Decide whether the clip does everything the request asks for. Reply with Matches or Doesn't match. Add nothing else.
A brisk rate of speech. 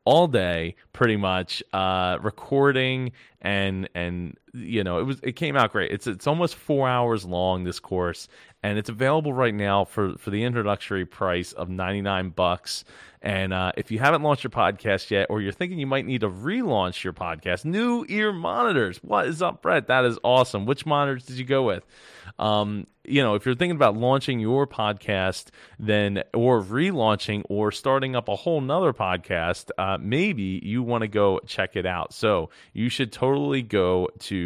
Doesn't match